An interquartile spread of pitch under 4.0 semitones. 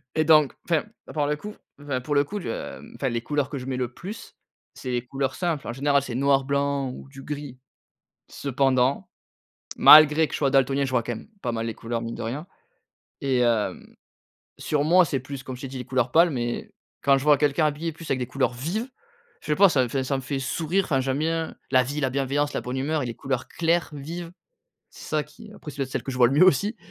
Yes: average, 3.0 semitones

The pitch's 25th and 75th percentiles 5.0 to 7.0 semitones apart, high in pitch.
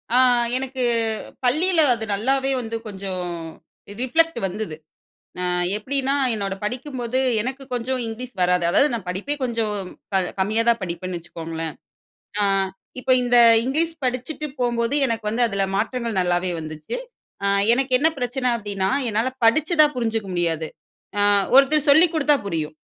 Yes: wide, 5.5 semitones; high, 235 Hz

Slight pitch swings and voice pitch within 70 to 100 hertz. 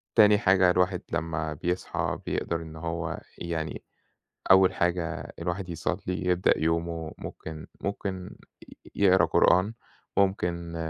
Yes: narrow, 2.1 semitones; very low, 90 Hz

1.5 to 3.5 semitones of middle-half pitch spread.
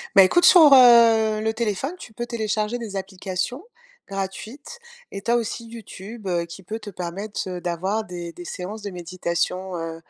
No: average, 3.9 semitones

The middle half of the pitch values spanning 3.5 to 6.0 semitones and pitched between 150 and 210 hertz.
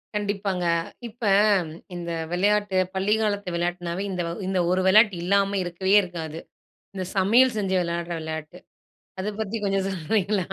No: average, 2.7 semitones; high, 190 Hz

